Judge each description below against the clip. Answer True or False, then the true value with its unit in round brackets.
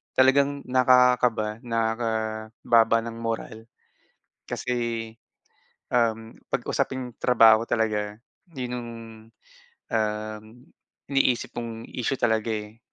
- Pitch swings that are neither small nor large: False (2.0 semitones)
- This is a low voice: True (115 Hz)